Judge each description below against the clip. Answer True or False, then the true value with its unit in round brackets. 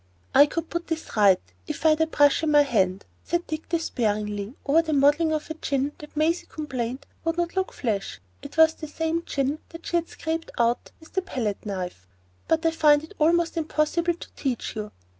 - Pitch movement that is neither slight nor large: False (5.8 semitones)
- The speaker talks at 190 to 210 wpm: True (195 wpm)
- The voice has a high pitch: True (300 Hz)